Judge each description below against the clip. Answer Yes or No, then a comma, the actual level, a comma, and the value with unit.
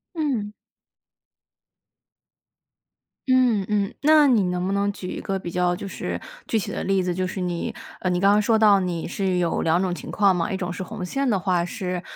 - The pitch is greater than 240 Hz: No, high, 190 Hz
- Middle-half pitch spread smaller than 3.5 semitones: Yes, average, 2.8 semitones